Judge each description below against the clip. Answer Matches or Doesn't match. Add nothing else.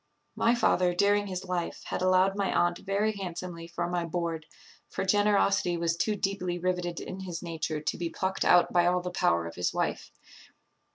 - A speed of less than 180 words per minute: Doesn't match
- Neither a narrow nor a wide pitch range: Doesn't match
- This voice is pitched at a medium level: Matches